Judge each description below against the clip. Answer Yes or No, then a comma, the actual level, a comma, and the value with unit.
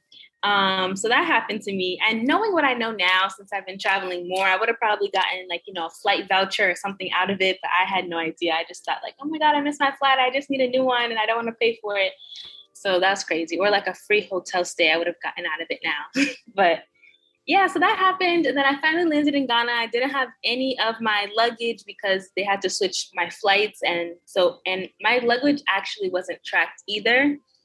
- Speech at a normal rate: No, fast, 250 wpm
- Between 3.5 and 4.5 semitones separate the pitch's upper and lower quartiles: No, wide, 5.6 semitones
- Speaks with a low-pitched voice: No, high, 205 Hz